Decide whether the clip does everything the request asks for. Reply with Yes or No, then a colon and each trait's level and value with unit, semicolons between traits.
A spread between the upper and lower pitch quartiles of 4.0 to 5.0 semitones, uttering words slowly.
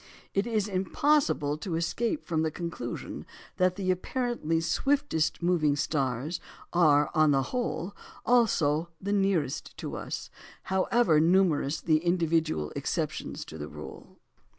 Yes: average, 4.3 semitones; slow, 130 wpm